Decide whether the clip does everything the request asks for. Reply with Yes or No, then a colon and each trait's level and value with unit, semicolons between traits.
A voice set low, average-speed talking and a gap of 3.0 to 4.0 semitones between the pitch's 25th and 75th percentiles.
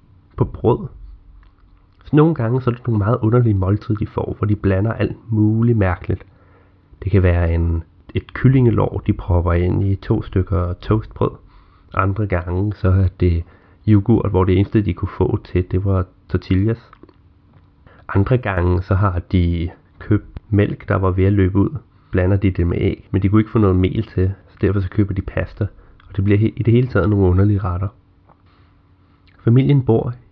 No: very low, 95 Hz; average, 185 wpm; narrow, 2.5 semitones